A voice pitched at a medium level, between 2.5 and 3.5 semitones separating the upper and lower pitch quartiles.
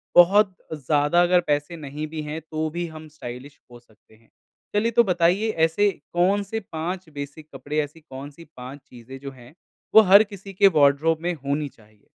No: medium, 155 Hz; average, 4.0 semitones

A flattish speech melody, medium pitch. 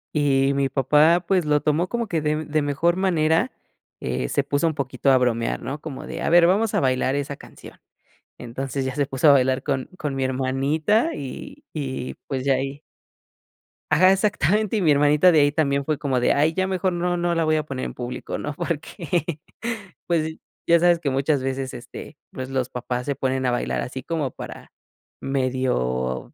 No: average, 4.0 semitones; medium, 145 Hz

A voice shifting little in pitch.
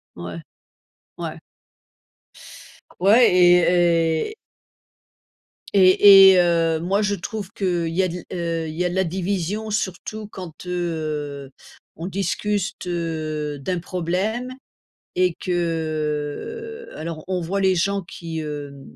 No: average, 3.2 semitones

